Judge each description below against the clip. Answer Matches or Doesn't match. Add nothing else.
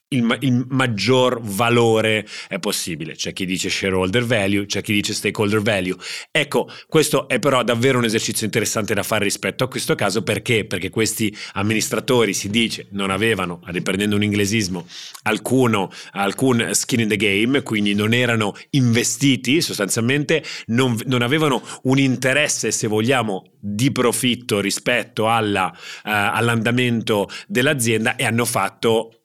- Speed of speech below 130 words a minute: Doesn't match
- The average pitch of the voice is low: Matches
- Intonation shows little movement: Doesn't match